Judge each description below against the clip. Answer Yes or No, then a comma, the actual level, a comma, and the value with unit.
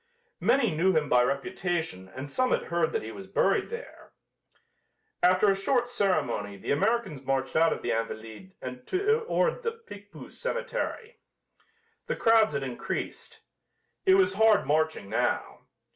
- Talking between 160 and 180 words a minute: No, average, 145 wpm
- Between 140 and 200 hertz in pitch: Yes, medium, 185 Hz